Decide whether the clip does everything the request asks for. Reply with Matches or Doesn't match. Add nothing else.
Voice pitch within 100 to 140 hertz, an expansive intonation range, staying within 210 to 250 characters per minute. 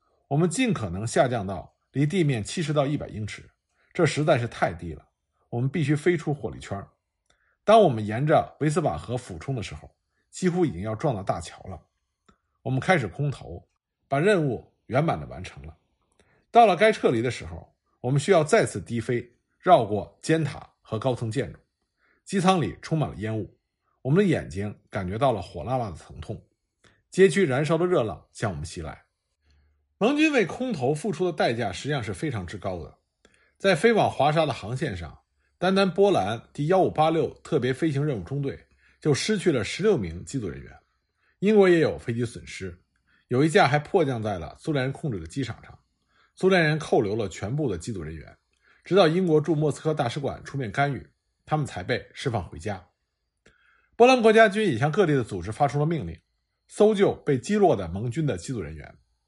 Doesn't match